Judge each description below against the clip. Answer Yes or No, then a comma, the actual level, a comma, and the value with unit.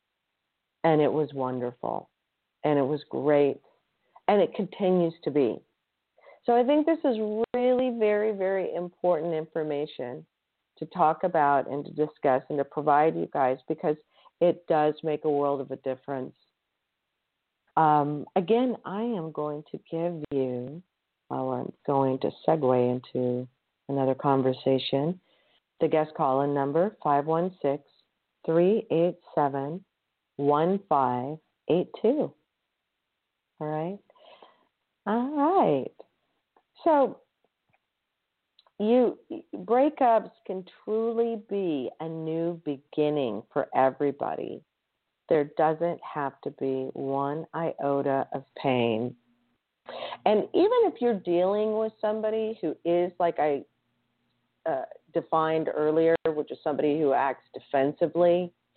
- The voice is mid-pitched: Yes, medium, 155 Hz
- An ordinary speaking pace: No, slow, 115 wpm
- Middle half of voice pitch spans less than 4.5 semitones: No, average, 5.1 semitones